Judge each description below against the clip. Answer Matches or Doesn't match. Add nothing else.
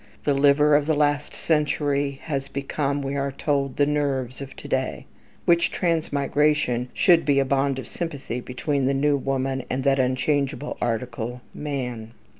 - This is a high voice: Doesn't match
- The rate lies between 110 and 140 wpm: Doesn't match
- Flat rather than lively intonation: Matches